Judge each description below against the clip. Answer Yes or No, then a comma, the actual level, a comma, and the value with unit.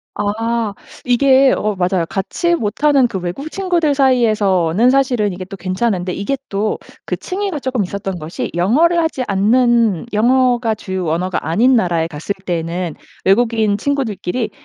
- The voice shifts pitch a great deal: Yes, wide, 5.7 semitones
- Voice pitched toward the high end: Yes, high, 215 Hz